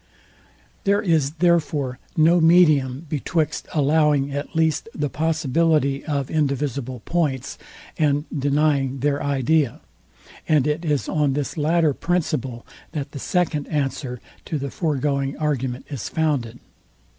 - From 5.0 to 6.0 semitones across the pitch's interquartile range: No, narrow, 2.6 semitones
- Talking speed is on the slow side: Yes, slow, 120 wpm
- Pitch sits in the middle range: Yes, medium, 145 Hz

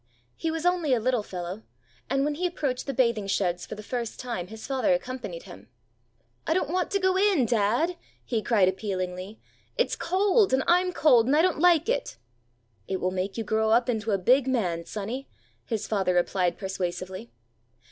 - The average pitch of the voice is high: Yes, high, 235 Hz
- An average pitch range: No, wide, 7.8 semitones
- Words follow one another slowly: No, average, 190 wpm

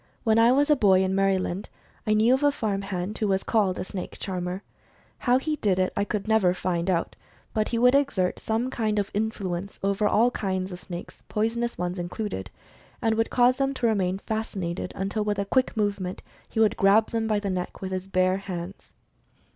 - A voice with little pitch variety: No, average, 3.2 semitones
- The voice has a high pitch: Yes, high, 200 Hz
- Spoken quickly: Yes, fast, 210 wpm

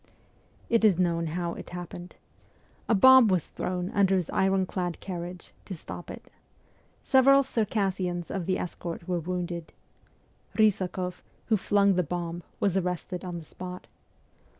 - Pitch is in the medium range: Yes, medium, 180 Hz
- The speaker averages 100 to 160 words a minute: Yes, average, 150 wpm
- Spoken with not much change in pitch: Yes, narrow, 2.0 semitones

